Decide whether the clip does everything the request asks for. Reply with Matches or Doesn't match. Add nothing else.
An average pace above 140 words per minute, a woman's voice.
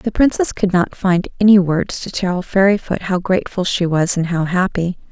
Matches